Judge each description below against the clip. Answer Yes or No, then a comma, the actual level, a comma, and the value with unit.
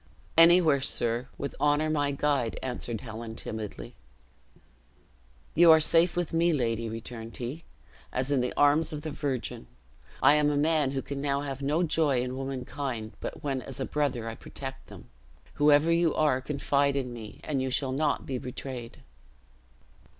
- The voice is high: No, medium, 140 Hz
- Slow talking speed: No, average, 165 wpm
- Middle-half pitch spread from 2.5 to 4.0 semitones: Yes, average, 3.1 semitones